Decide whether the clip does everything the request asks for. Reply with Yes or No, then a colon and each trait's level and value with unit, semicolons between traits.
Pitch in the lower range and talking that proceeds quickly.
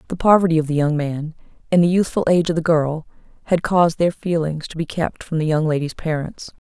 No: medium, 160 Hz; fast, 225 wpm